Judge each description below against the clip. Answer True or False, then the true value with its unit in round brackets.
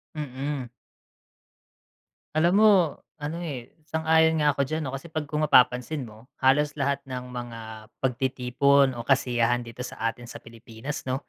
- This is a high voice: False (135 Hz)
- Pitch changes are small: False (3.4 semitones)